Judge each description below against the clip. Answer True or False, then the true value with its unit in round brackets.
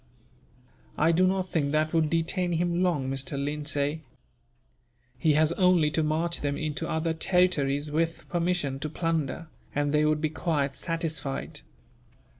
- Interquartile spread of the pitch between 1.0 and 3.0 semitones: True (2.5 semitones)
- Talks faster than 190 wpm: False (145 wpm)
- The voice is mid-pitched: True (155 Hz)